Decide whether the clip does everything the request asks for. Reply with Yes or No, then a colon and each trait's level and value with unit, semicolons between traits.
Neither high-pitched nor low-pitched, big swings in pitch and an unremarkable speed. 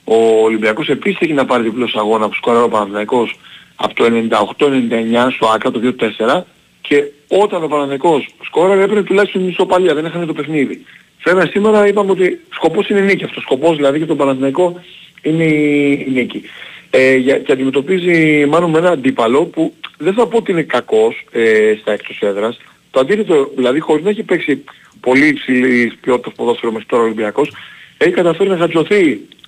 No: medium, 150 Hz; wide, 6.6 semitones; fast, 175 wpm